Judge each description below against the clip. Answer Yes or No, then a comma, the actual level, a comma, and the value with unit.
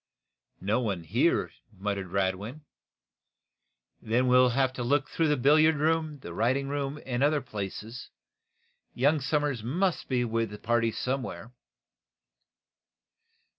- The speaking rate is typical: No, slow, 110 wpm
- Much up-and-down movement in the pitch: No, average, 4.6 semitones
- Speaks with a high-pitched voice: No, low, 125 Hz